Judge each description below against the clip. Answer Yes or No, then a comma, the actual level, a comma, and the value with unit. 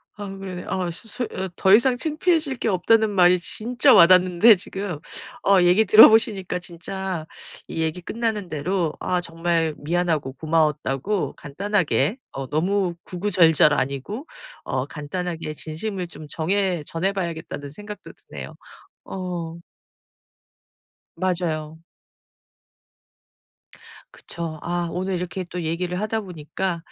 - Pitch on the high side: No, medium, 180 Hz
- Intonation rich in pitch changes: No, average, 3.5 semitones